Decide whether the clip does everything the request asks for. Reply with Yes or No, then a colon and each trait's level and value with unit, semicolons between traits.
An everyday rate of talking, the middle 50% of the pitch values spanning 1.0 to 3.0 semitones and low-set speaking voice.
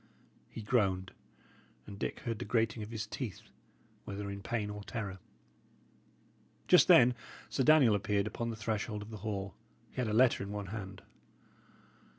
Yes: average, 160 wpm; narrow, 2.4 semitones; low, 105 Hz